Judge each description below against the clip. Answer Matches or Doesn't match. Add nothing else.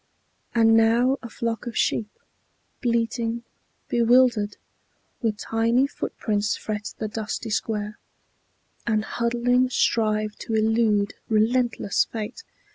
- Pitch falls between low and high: Doesn't match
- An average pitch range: Doesn't match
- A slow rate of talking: Matches